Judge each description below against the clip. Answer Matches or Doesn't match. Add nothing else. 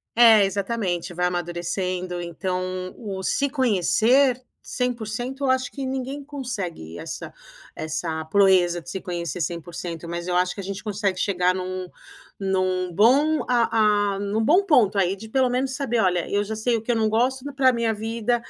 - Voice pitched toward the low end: Doesn't match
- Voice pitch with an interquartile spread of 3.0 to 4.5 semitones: Doesn't match